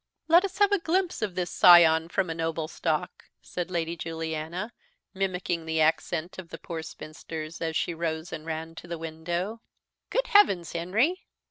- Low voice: No, medium, 170 Hz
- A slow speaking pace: No, average, 170 wpm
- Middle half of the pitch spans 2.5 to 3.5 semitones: Yes, average, 2.8 semitones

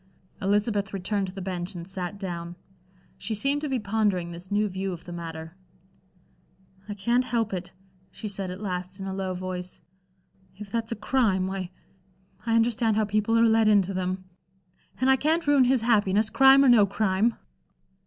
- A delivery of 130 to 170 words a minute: No, average, 180 wpm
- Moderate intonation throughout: Yes, average, 3.5 semitones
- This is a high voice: Yes, high, 200 Hz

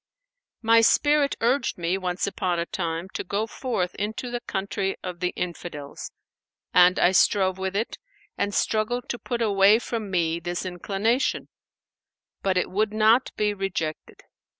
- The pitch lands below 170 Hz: No, high, 195 Hz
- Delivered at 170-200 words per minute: No, average, 150 wpm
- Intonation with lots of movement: No, average, 3.6 semitones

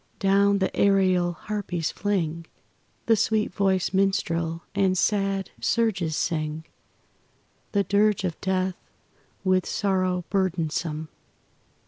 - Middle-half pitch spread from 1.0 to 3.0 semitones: Yes, narrow, 2.6 semitones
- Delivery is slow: Yes, slow, 100 wpm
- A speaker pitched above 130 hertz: Yes, high, 190 Hz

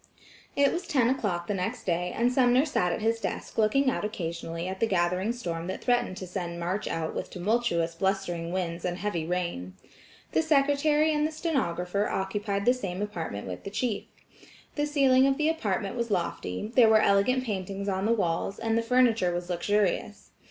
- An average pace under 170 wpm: No, average, 185 wpm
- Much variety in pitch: Yes, wide, 5.7 semitones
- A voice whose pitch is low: No, high, 200 Hz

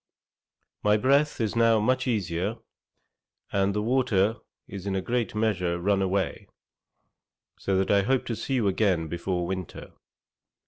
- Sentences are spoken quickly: No, average, 145 wpm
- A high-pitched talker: No, low, 100 Hz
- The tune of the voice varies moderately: Yes, average, 3.5 semitones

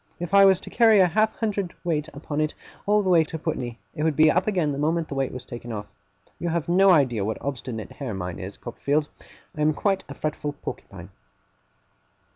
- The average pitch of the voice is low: No, medium, 155 Hz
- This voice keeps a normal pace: No, fast, 215 wpm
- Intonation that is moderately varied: No, wide, 5.7 semitones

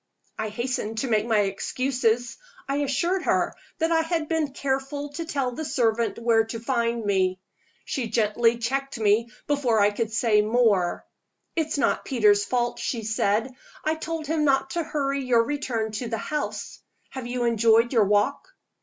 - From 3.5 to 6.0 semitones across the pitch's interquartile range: Yes, average, 3.9 semitones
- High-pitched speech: Yes, high, 240 Hz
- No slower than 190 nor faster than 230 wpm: No, average, 170 wpm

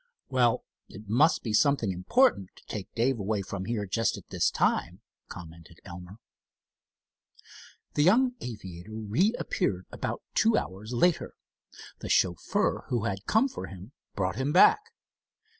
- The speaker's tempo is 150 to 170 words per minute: No, average, 140 wpm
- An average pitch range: No, wide, 6.8 semitones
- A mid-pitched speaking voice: No, low, 110 Hz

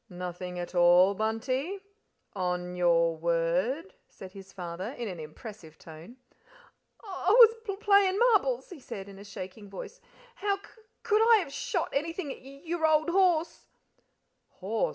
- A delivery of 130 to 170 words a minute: Yes, average, 160 wpm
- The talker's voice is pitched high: Yes, high, 230 Hz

